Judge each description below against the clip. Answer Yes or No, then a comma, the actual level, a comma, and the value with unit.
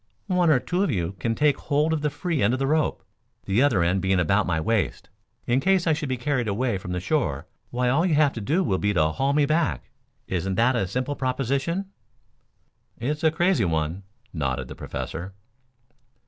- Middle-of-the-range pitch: No, low, 130 Hz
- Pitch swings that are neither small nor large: No, wide, 7.8 semitones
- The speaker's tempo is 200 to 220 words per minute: Yes, fast, 205 wpm